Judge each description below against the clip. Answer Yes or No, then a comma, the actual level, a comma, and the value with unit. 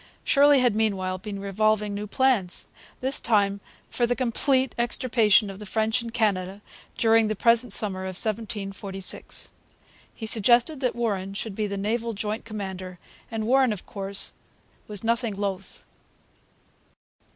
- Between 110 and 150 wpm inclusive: Yes, average, 140 wpm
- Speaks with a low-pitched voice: No, high, 215 Hz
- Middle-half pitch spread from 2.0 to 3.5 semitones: Yes, average, 3.0 semitones